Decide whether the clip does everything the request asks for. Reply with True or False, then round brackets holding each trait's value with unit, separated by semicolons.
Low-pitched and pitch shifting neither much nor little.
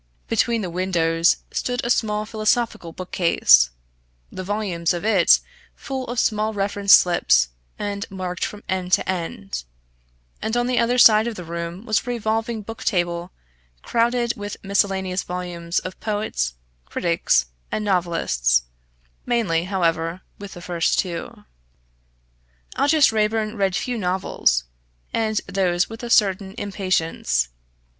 False (195 Hz; 4.1 semitones)